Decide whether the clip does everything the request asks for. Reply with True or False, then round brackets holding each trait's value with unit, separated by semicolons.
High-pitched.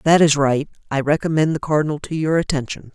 False (150 Hz)